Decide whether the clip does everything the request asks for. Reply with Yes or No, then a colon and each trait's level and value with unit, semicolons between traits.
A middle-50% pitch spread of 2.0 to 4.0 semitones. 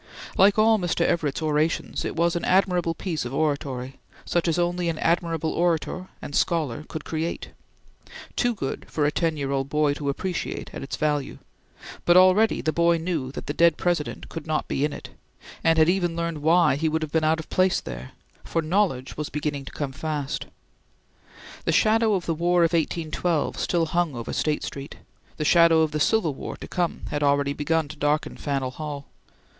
Yes: average, 2.8 semitones